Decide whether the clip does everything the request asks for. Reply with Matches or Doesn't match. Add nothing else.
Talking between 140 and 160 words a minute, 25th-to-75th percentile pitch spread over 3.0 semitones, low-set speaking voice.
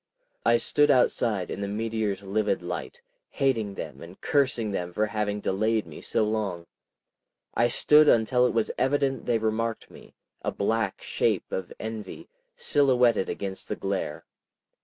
Matches